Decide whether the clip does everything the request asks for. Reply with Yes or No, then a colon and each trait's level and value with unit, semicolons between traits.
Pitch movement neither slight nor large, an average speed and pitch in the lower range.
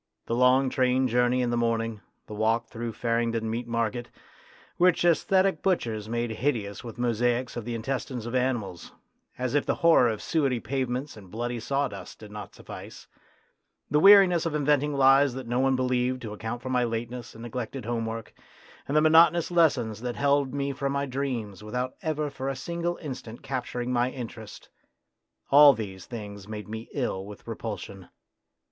Yes: average, 3.3 semitones; average, 170 wpm; low, 125 Hz